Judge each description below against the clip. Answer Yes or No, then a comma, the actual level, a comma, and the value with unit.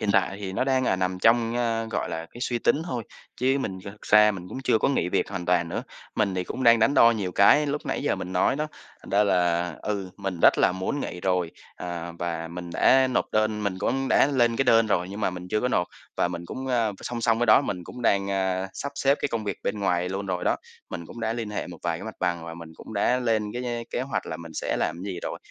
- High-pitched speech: No, low, 100 Hz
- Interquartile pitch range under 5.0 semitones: Yes, average, 4.6 semitones